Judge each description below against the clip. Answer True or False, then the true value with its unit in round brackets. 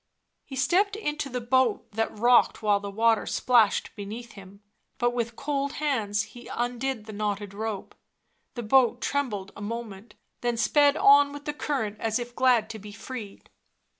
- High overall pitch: True (235 Hz)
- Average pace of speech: True (165 wpm)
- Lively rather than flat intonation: False (3.9 semitones)